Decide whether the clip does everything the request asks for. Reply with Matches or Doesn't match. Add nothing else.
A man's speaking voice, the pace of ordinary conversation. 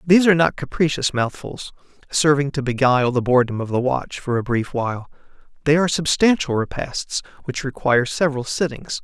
Matches